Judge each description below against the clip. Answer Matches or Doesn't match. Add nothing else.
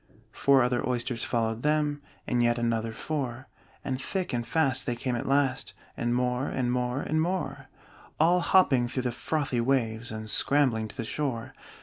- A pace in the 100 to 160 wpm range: Doesn't match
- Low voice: Matches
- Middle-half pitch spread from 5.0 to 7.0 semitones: Doesn't match